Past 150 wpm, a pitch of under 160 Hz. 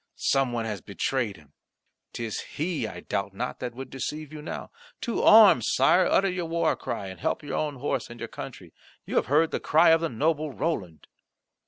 Yes: average, 200 wpm; low, 135 Hz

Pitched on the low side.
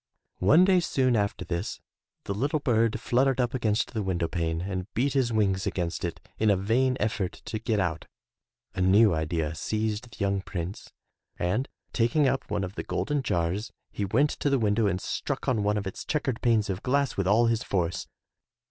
Yes: low, 105 Hz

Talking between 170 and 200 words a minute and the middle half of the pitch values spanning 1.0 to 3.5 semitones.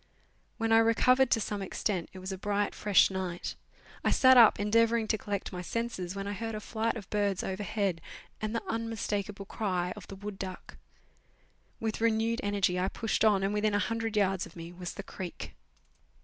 Yes: average, 190 wpm; average, 2.8 semitones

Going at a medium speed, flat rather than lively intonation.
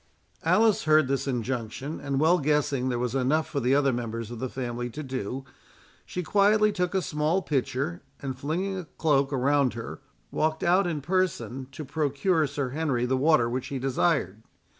No: average, 180 wpm; average, 3.8 semitones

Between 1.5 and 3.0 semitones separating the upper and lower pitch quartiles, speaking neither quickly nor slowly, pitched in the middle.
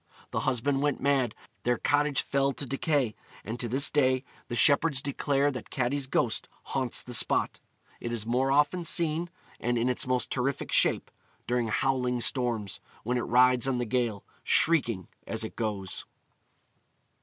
No: average, 2.7 semitones; average, 160 wpm; low, 125 Hz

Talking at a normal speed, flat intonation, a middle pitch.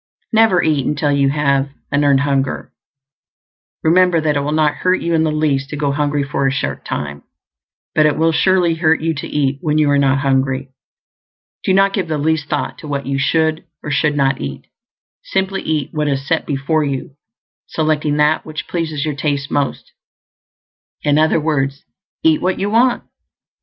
Yes: average, 185 wpm; narrow, 2.3 semitones; medium, 150 Hz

